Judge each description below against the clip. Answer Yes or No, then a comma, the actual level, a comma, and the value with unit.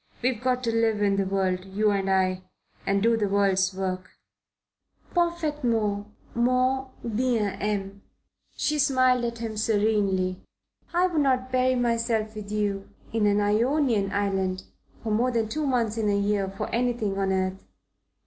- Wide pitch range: No, average, 3.9 semitones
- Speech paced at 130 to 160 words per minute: Yes, average, 155 wpm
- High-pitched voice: Yes, high, 215 Hz